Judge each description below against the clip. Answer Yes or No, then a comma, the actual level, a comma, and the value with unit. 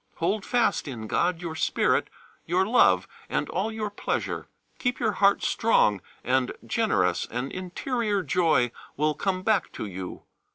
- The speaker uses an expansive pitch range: Yes, wide, 8.5 semitones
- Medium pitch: Yes, medium, 180 Hz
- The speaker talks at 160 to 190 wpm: No, average, 150 wpm